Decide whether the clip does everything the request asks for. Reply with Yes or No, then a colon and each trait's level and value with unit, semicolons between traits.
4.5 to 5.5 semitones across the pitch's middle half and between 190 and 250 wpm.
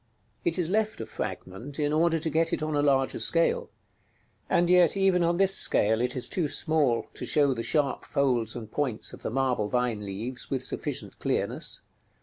Yes: average, 5.2 semitones; average, 200 wpm